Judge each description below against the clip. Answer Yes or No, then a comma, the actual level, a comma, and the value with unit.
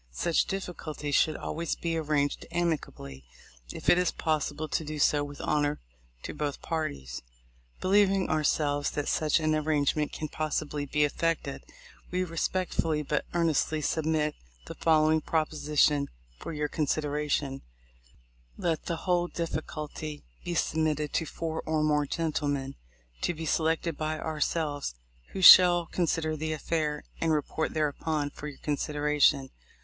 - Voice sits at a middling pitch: Yes, medium, 155 Hz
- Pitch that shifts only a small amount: Yes, narrow, 1.8 semitones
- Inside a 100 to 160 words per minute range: Yes, average, 140 wpm